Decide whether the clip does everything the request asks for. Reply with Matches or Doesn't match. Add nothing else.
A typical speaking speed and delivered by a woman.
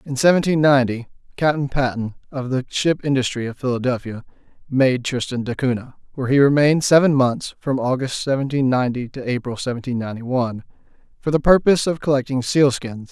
Doesn't match